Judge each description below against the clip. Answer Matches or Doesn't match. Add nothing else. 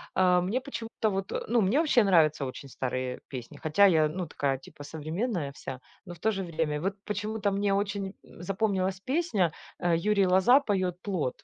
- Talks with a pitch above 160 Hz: Matches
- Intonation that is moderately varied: Matches